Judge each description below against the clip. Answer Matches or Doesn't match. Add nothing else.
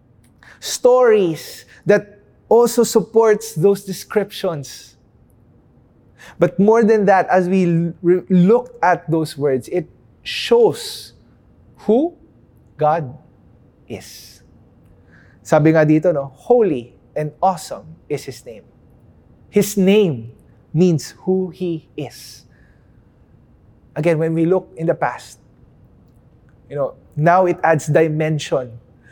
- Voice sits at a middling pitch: Matches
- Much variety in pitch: Matches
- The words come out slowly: Matches